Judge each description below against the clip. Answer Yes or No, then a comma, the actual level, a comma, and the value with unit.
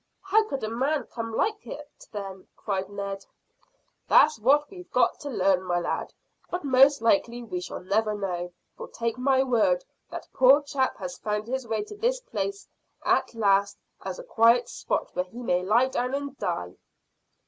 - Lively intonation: Yes, wide, 6.1 semitones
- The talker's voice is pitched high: Yes, high, 235 Hz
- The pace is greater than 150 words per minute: Yes, average, 180 wpm